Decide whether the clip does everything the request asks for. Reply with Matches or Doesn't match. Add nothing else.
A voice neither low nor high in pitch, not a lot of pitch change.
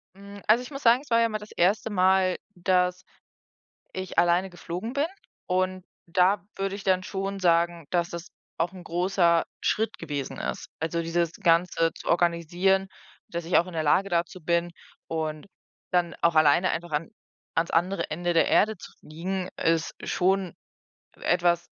Matches